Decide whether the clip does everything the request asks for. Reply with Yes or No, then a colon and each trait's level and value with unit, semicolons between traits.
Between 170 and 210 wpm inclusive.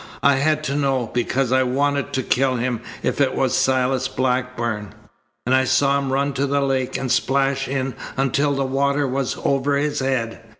Yes: average, 185 wpm